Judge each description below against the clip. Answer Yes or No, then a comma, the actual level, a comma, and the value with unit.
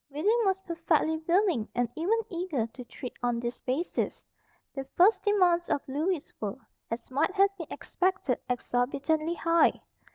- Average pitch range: No, wide, 6.4 semitones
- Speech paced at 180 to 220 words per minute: No, average, 150 wpm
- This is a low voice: No, very high, 320 Hz